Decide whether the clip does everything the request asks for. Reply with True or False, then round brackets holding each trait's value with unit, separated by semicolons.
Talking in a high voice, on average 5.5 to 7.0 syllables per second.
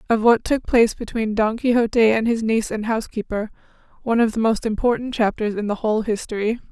True (225 Hz; 6.3 syllables/s)